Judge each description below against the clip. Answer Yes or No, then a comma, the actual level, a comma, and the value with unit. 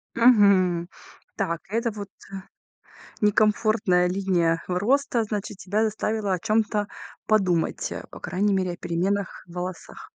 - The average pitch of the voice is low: No, high, 200 Hz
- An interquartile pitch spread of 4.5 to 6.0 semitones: No, average, 3.1 semitones